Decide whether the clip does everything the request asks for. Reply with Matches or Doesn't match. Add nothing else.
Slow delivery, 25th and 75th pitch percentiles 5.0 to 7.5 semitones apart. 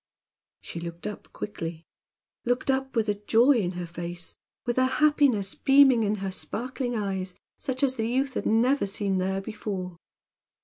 Doesn't match